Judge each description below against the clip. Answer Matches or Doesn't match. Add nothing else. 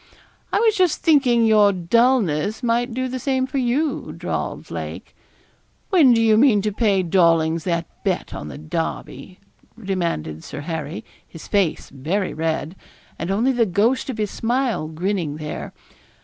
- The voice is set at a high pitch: Matches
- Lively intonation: Matches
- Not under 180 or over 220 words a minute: Doesn't match